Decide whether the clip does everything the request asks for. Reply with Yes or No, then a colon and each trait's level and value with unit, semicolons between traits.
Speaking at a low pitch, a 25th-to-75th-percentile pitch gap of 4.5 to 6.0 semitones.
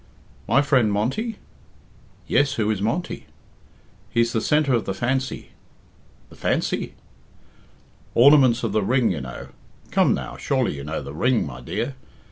Yes: low, 115 Hz; average, 5.1 semitones